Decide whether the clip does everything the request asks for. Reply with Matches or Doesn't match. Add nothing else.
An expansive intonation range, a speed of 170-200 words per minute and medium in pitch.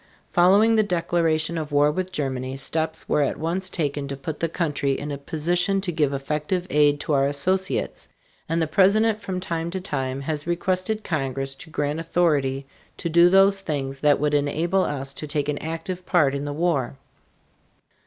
Doesn't match